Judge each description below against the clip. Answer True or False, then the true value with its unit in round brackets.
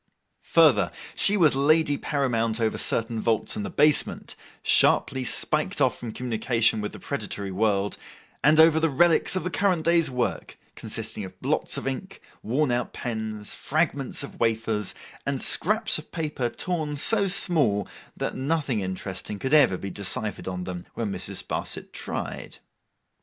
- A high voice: False (125 Hz)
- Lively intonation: True (6.2 semitones)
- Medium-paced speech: True (155 wpm)